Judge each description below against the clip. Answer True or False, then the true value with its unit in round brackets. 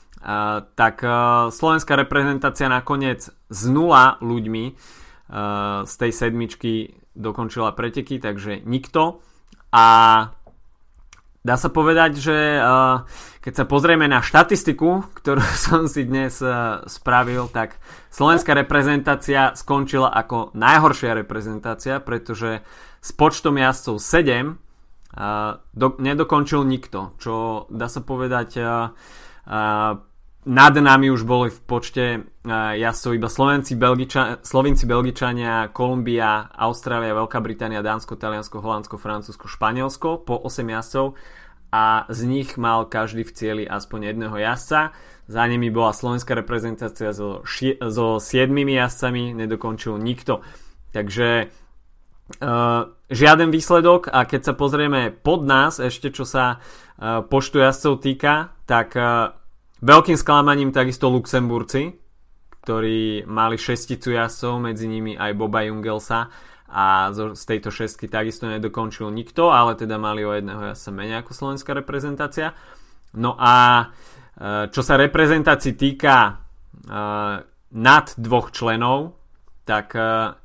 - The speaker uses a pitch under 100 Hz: False (120 Hz)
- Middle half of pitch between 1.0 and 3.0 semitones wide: False (3.4 semitones)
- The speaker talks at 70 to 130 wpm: True (125 wpm)